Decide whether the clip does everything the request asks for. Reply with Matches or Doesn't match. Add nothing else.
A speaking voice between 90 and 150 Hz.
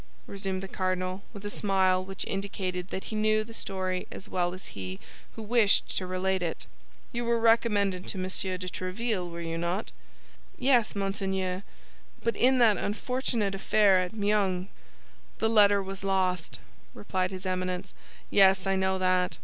Doesn't match